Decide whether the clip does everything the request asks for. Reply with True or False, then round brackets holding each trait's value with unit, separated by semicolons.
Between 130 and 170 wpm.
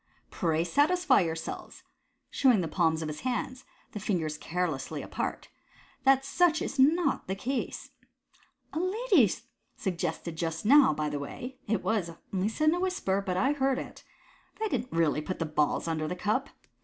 False (180 wpm)